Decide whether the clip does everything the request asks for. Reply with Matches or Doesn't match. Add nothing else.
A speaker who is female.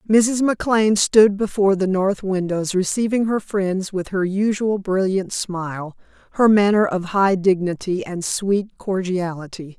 Matches